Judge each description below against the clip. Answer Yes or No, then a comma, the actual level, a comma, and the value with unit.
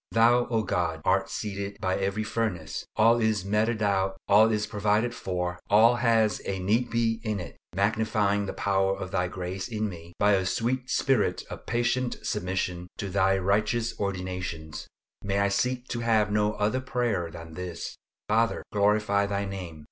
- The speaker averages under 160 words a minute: No, average, 170 wpm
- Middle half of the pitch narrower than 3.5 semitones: Yes, average, 3.0 semitones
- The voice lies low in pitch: Yes, low, 105 Hz